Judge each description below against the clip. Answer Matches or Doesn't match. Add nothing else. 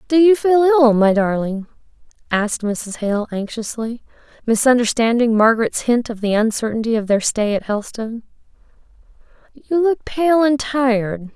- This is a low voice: Doesn't match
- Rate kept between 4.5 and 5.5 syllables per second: Matches